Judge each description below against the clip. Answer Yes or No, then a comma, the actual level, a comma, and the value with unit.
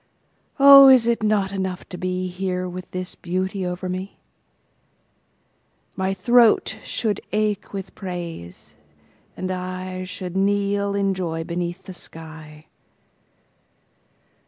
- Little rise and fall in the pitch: Yes, narrow, 1.9 semitones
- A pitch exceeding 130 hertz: Yes, medium, 185 Hz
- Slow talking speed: Yes, slow, 105 wpm